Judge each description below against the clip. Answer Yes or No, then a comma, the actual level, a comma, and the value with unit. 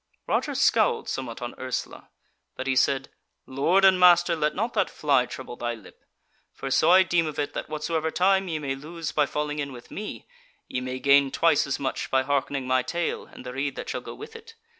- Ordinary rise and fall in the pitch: Yes, average, 4.4 semitones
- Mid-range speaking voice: Yes, medium, 145 Hz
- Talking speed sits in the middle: No, fast, 220 wpm